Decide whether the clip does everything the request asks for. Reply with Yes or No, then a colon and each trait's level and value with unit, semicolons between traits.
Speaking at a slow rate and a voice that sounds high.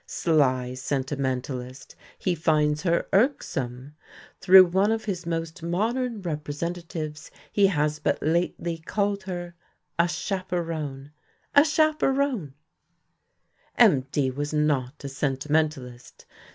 No: slow, 100 wpm; medium, 160 Hz